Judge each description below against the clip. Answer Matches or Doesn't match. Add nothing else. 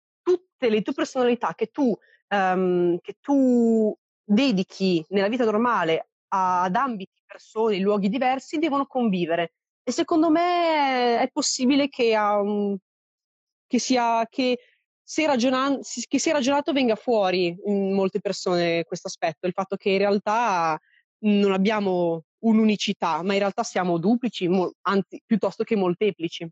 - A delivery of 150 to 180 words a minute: Doesn't match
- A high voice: Matches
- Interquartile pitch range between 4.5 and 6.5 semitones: Matches